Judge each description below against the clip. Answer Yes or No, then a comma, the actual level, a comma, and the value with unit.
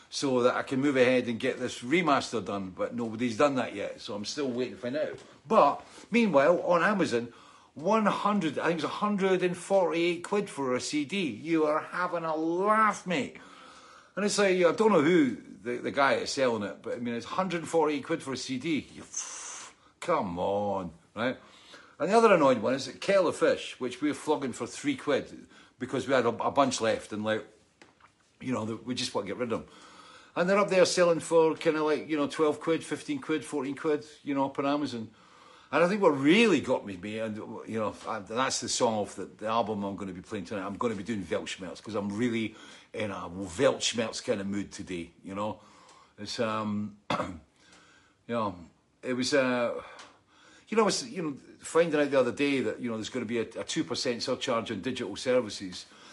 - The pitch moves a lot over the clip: Yes, wide, 7.4 semitones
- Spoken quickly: Yes, fast, 220 wpm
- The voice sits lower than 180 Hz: Yes, medium, 140 Hz